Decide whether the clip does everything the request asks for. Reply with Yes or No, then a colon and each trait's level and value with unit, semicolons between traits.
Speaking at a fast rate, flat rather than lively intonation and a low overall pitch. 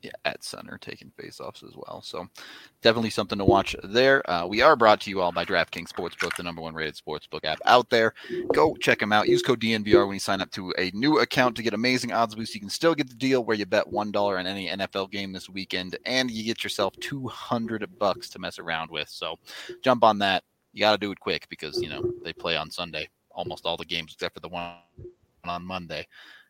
No: fast, 240 wpm; average, 4.6 semitones; low, 105 Hz